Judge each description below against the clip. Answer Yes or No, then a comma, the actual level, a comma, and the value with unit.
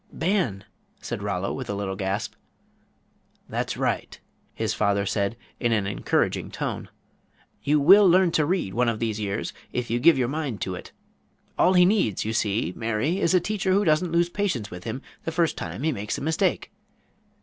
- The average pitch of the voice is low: Yes, low, 120 Hz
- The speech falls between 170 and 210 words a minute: Yes, average, 185 wpm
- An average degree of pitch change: No, wide, 8.8 semitones